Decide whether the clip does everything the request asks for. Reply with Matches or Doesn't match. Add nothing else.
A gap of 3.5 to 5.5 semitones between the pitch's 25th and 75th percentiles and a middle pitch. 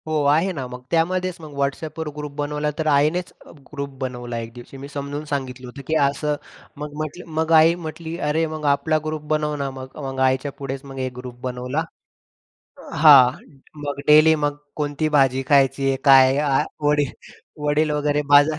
Doesn't match